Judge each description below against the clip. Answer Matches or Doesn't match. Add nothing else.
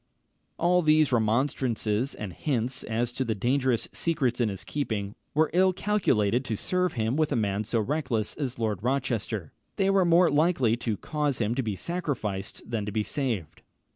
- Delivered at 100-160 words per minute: Doesn't match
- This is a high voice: Doesn't match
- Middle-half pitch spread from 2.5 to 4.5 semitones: Doesn't match